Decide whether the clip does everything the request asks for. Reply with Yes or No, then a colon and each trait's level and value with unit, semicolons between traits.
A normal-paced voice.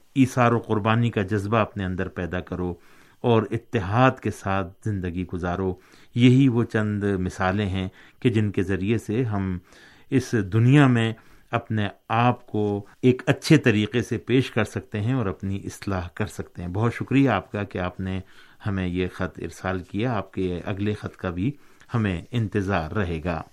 Yes: average, 175 wpm